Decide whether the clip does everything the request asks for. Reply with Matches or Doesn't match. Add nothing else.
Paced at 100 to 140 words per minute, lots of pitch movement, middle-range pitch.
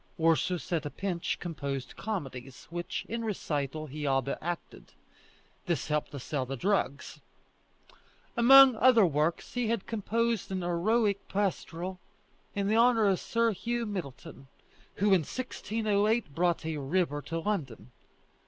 Matches